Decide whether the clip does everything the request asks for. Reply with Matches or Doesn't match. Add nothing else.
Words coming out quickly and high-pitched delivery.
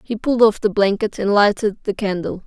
Matches